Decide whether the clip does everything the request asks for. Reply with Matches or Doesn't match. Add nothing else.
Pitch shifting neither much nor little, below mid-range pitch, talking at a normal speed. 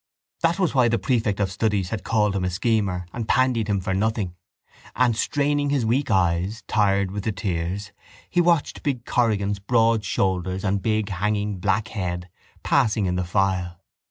Matches